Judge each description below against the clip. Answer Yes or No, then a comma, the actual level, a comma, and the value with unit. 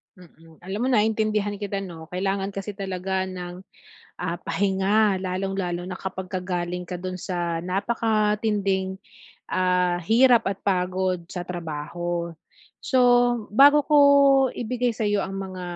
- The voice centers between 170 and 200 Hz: Yes, high, 190 Hz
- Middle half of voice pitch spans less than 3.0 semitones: Yes, narrow, 2.5 semitones